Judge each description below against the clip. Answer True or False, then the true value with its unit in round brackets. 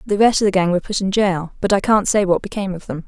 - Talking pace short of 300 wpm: False (330 wpm)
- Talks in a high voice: True (195 Hz)